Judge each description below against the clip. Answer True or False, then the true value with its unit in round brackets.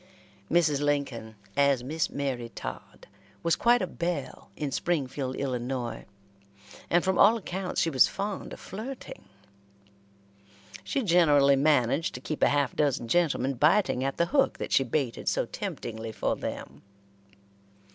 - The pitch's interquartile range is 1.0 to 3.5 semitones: False (5.0 semitones)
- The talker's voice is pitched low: False (145 Hz)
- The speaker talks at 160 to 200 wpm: False (140 wpm)